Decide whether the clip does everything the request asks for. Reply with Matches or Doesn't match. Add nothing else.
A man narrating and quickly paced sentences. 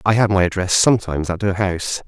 Matches